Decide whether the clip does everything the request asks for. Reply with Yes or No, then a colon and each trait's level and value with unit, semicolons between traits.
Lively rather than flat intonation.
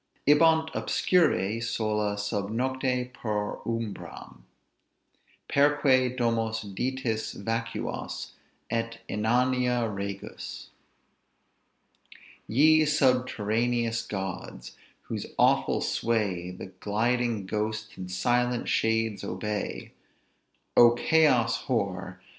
No: average, 3.3 semitones